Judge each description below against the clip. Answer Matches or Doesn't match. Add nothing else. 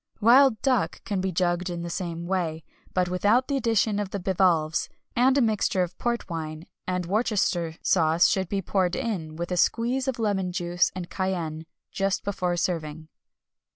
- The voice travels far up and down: Doesn't match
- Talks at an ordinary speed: Matches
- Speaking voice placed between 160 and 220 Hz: Matches